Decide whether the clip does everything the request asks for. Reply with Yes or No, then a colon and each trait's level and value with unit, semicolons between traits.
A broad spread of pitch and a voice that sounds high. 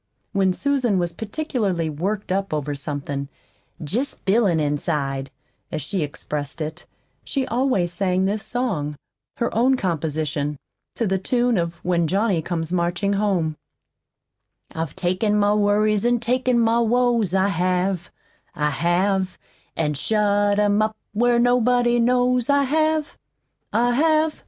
Yes: wide, 6.0 semitones; high, 200 Hz